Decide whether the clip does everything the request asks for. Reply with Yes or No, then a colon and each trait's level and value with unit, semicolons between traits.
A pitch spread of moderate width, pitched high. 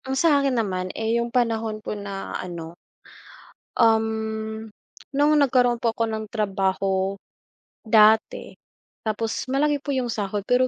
Yes: average, 3.2 semitones; high, 220 Hz